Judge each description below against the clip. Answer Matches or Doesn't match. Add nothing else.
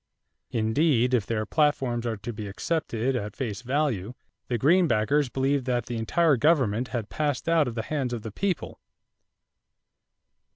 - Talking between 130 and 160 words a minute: Matches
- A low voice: Matches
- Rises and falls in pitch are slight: Doesn't match